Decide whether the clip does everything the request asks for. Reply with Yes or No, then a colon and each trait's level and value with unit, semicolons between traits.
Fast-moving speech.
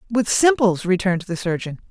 No: average, 155 wpm